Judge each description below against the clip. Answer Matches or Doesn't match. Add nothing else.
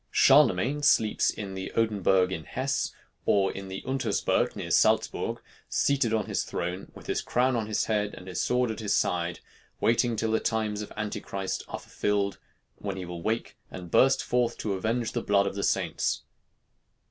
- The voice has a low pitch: Matches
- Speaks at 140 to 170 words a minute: Doesn't match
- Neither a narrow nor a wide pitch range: Matches